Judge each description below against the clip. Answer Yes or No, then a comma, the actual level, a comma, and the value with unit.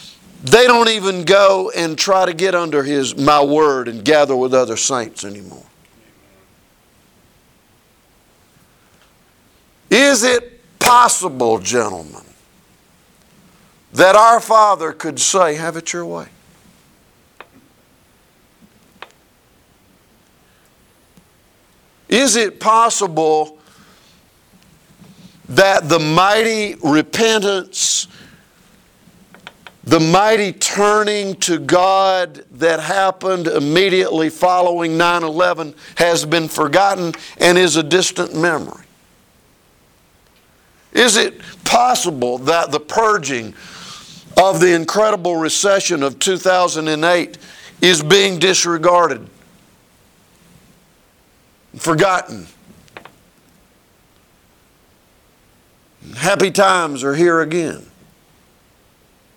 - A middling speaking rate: No, slow, 80 wpm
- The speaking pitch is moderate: Yes, medium, 175 Hz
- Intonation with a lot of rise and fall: No, average, 3.8 semitones